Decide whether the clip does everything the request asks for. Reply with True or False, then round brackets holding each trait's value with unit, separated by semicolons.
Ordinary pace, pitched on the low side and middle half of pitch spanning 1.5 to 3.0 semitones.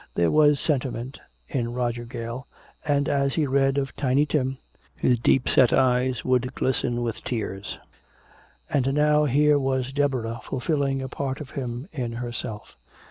True (145 wpm; 130 Hz; 2.7 semitones)